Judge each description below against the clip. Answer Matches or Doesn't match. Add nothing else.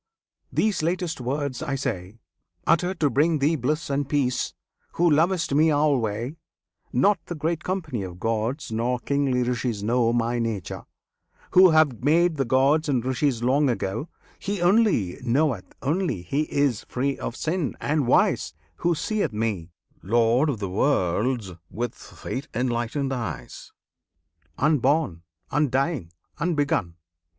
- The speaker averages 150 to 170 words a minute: Doesn't match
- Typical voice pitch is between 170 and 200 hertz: Doesn't match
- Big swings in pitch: Doesn't match